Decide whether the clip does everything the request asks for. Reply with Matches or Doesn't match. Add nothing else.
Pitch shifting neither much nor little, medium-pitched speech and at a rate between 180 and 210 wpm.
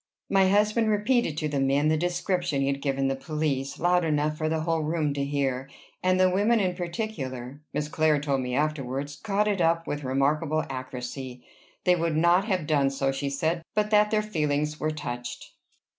Matches